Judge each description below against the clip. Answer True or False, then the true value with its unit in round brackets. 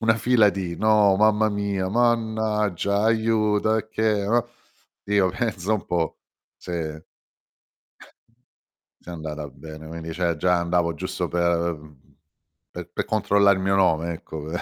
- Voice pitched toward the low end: True (95 Hz)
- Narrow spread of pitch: False (4.1 semitones)